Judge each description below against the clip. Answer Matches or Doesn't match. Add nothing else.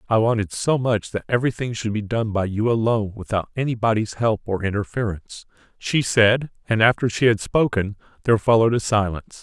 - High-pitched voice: Doesn't match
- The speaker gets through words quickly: Doesn't match